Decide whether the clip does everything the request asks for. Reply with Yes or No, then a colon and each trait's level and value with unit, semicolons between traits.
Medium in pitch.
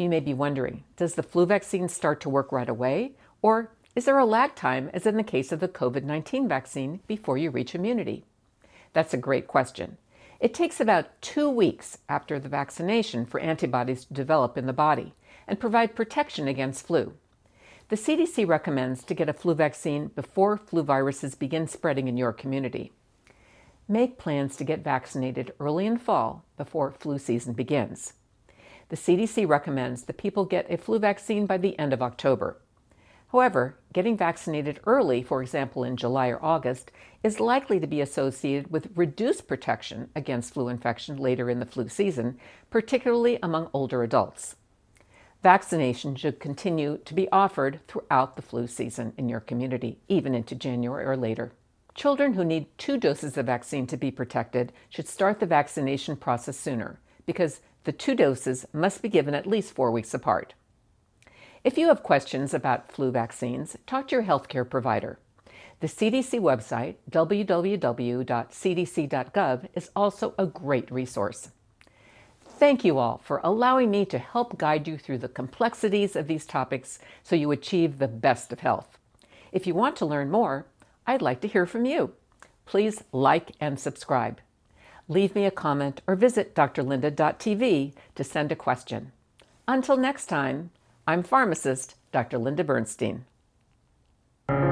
Yes: medium, 150 Hz